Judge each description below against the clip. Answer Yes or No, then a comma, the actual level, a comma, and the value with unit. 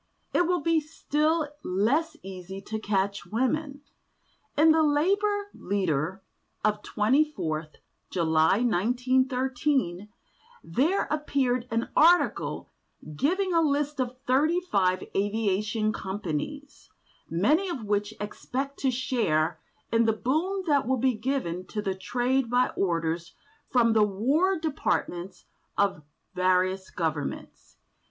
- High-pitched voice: Yes, high, 240 Hz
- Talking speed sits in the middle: No, slow, 115 wpm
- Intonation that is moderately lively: No, wide, 7.4 semitones